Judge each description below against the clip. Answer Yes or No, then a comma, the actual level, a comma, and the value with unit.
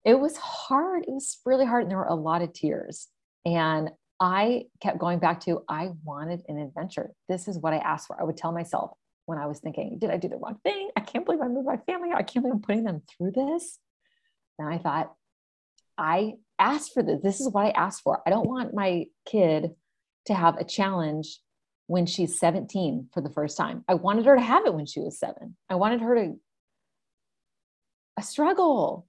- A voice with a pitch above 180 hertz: Yes, high, 190 Hz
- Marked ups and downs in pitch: Yes, wide, 6.5 semitones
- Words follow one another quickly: Yes, fast, 215 wpm